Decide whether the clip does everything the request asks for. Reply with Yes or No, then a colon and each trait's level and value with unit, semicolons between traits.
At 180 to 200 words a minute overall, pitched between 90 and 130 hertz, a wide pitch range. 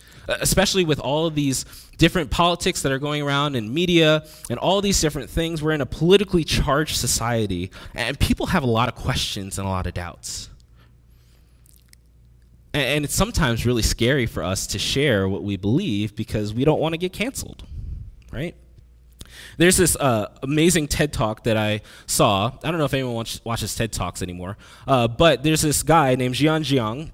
Yes: average, 185 wpm; low, 125 Hz; wide, 7.6 semitones